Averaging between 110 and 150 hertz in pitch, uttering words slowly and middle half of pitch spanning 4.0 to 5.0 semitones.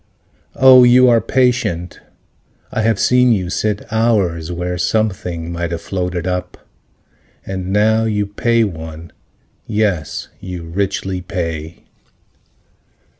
No: very low, 95 Hz; slow, 115 wpm; average, 4.3 semitones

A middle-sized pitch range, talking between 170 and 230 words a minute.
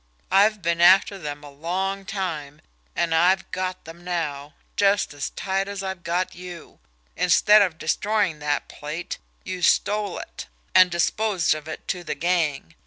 No: average, 3.4 semitones; average, 160 wpm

